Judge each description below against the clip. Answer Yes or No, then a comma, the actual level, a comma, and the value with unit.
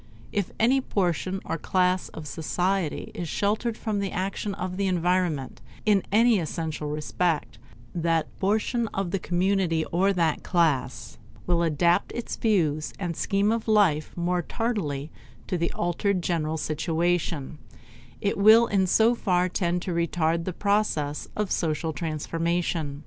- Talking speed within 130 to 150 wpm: Yes, average, 145 wpm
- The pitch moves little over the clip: No, average, 3.5 semitones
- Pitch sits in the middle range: Yes, medium, 175 Hz